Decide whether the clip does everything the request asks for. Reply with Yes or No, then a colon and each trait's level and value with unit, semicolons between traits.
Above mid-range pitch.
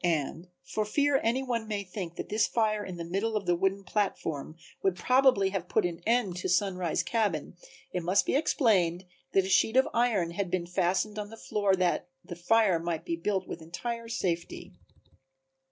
Yes: high, 195 Hz